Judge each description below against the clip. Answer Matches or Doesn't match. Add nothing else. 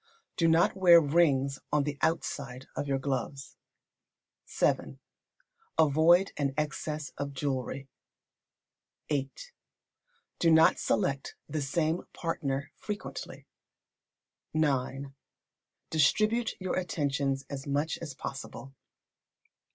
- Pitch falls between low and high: Matches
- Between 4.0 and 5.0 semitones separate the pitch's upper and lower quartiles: Doesn't match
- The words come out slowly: Matches